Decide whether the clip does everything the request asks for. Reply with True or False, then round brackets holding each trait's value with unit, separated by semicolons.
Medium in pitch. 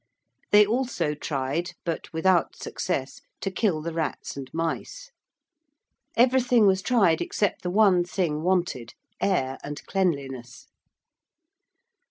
True (175 Hz)